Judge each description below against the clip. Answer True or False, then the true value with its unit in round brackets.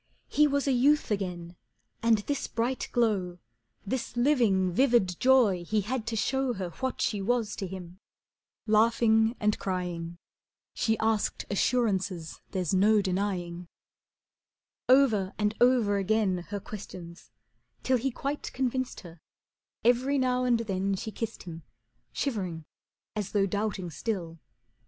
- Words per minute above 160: False (135 wpm)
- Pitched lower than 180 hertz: False (210 Hz)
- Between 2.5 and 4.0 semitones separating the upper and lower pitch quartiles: False (4.6 semitones)